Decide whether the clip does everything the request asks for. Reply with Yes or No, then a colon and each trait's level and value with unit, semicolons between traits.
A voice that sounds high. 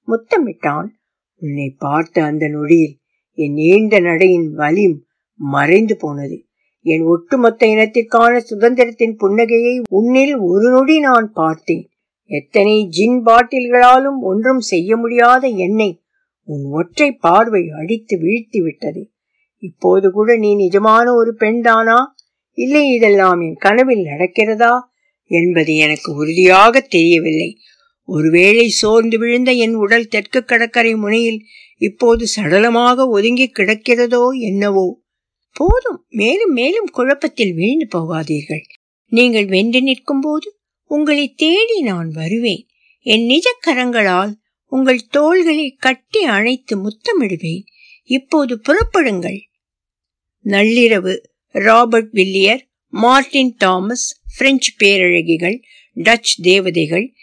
Yes: high, 225 Hz